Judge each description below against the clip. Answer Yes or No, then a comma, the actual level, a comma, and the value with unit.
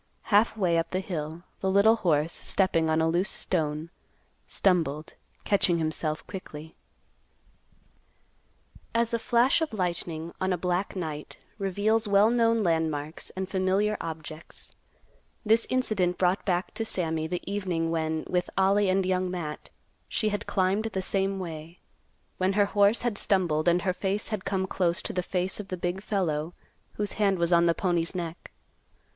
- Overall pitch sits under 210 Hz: Yes, medium, 185 Hz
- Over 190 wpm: No, average, 160 wpm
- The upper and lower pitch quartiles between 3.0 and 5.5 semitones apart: Yes, average, 3.3 semitones